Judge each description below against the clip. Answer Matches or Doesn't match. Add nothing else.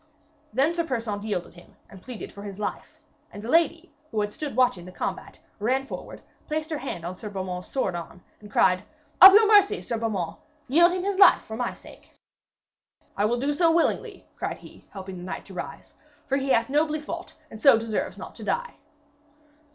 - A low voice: Doesn't match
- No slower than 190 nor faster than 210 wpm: Matches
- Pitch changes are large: Matches